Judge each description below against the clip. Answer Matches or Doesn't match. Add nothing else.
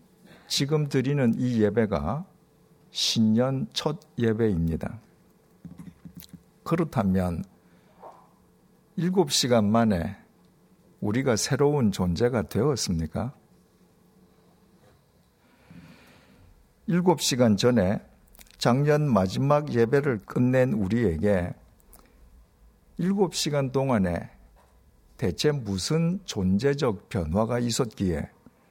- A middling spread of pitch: Doesn't match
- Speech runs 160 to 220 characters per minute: Matches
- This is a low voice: Matches